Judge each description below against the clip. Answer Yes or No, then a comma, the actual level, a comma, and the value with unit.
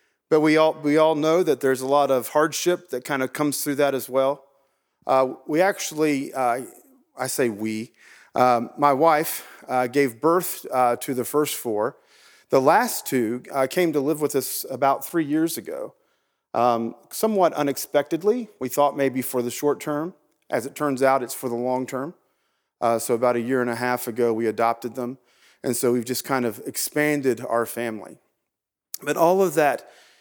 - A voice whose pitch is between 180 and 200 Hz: No, low, 135 Hz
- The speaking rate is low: No, average, 190 wpm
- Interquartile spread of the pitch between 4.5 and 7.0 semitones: No, average, 3.8 semitones